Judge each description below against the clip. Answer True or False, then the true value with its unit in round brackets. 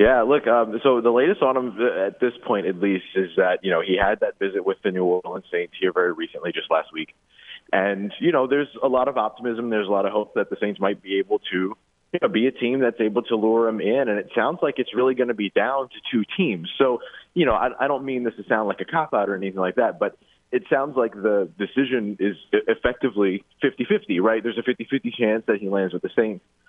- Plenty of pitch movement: False (4.6 semitones)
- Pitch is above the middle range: False (120 Hz)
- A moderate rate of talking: False (260 wpm)